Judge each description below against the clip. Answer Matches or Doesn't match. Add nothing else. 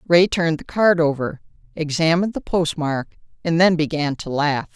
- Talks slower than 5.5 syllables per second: Matches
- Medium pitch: Matches